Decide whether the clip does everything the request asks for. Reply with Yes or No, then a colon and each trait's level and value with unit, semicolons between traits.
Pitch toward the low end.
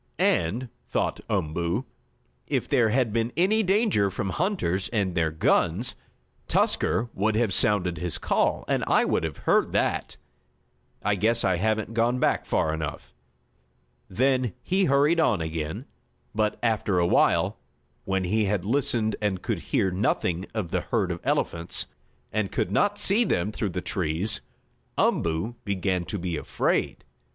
Yes: low, 105 Hz